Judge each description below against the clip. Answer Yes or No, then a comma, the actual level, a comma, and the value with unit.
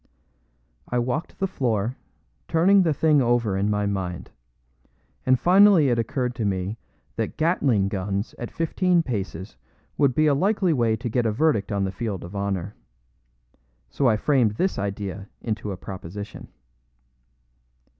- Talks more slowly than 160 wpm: Yes, average, 150 wpm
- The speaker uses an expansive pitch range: Yes, wide, 6.7 semitones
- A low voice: Yes, low, 115 Hz